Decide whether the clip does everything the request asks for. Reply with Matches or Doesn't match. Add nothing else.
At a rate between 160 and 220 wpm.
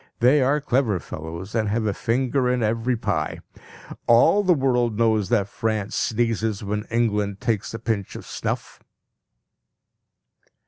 Doesn't match